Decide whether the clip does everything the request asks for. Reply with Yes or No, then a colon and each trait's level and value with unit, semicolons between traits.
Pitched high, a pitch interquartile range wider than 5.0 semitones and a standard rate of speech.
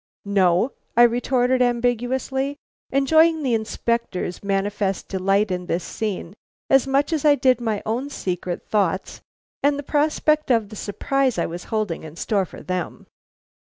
Yes: high, 230 Hz; wide, 5.6 semitones; average, 150 wpm